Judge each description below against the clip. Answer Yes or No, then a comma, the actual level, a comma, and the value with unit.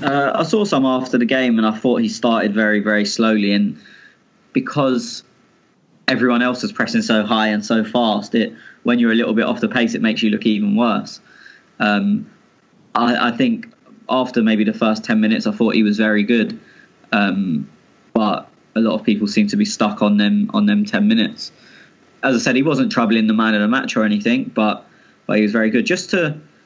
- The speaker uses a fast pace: Yes, fast, 210 wpm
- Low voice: Yes, low, 125 Hz